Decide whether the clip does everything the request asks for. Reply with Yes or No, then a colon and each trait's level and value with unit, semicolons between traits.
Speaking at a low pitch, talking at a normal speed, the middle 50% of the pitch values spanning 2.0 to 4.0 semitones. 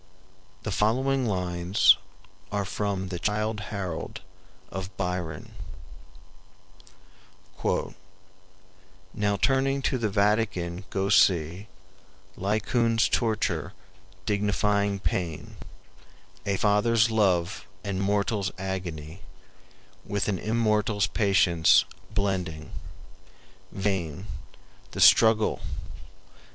No: low, 100 Hz; slow, 80 wpm; narrow, 2.6 semitones